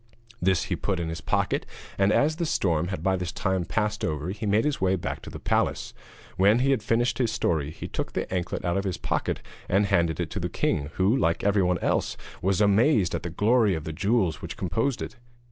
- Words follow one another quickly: Yes, fast, 230 wpm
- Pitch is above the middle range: No, very low, 95 Hz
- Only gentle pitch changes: No, average, 4.0 semitones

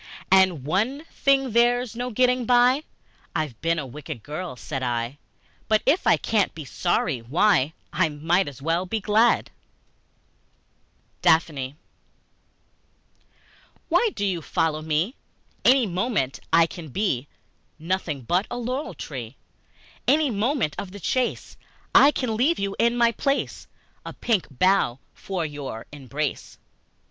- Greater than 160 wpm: No, slow, 135 wpm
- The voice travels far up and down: Yes, wide, 8.1 semitones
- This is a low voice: No, medium, 185 Hz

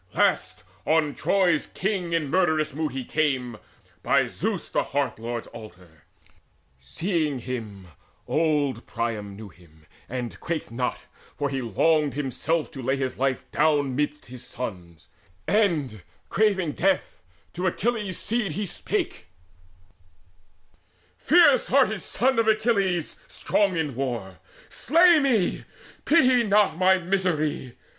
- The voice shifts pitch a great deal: Yes, wide, 7.3 semitones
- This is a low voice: No, medium, 155 Hz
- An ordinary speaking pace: No, slow, 125 wpm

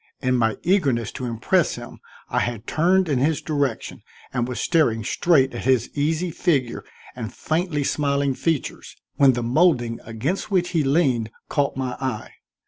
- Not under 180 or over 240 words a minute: No, average, 160 wpm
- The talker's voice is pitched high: No, low, 135 Hz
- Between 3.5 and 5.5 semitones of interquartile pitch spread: Yes, average, 5.0 semitones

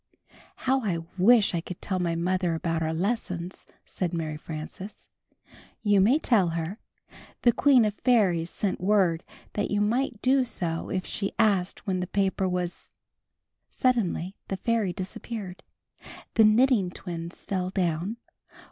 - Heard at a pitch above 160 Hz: Yes, high, 190 Hz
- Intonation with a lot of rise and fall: No, average, 3.8 semitones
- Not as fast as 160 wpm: Yes, average, 145 wpm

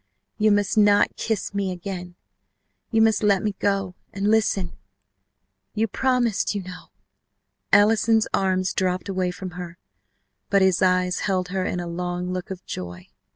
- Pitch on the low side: No, high, 190 Hz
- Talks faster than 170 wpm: No, average, 160 wpm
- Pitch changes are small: Yes, narrow, 2.3 semitones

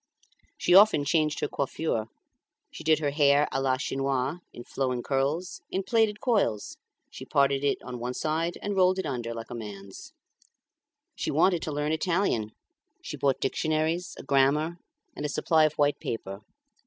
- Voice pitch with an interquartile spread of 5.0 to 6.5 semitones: No, average, 4.2 semitones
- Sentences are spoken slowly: No, average, 165 wpm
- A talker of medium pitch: Yes, medium, 145 Hz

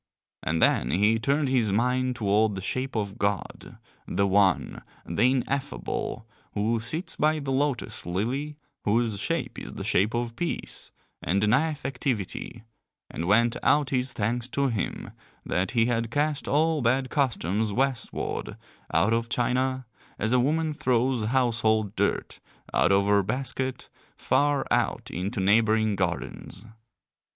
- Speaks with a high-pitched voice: No, low, 115 Hz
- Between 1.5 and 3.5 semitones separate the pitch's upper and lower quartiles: No, average, 4.4 semitones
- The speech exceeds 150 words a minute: No, average, 140 wpm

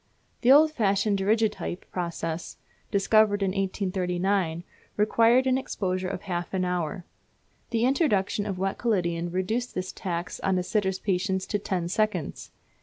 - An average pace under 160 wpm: Yes, average, 140 wpm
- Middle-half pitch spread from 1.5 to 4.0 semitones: Yes, average, 3.0 semitones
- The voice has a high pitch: Yes, high, 195 Hz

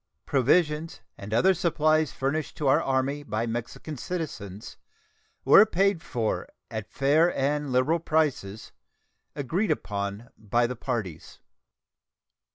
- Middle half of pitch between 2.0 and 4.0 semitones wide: No, wide, 5.5 semitones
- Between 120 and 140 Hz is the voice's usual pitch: Yes, low, 135 Hz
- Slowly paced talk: Yes, slow, 115 wpm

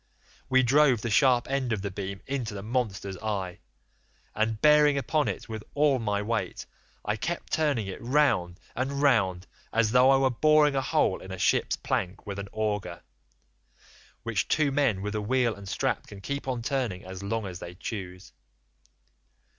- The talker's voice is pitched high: No, low, 115 Hz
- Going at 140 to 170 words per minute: No, average, 180 wpm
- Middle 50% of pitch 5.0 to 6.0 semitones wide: Yes, average, 5.3 semitones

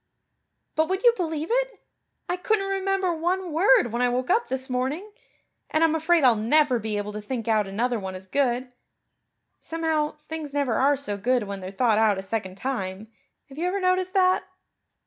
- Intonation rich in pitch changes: Yes, wide, 7.7 semitones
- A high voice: Yes, very high, 275 Hz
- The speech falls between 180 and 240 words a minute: Yes, average, 190 wpm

